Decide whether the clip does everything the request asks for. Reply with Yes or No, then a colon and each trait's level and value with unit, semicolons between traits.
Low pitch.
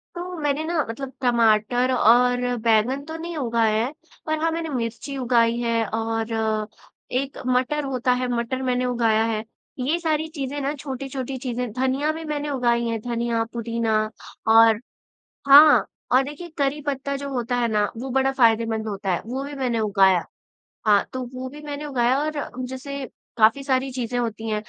No: very high, 250 Hz